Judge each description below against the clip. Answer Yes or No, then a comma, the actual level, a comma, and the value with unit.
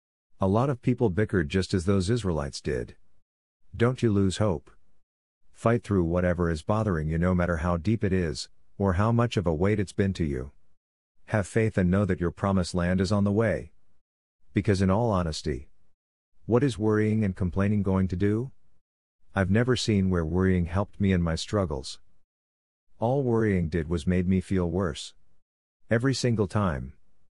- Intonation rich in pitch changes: No, average, 3.8 semitones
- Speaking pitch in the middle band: No, very low, 95 Hz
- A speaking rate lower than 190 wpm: Yes, average, 180 wpm